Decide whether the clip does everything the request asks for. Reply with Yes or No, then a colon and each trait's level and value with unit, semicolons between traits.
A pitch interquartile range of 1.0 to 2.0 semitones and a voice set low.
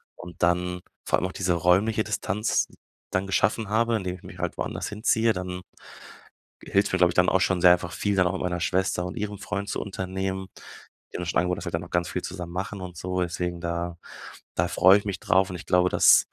Yes: narrow, 1.7 semitones; very low, 90 Hz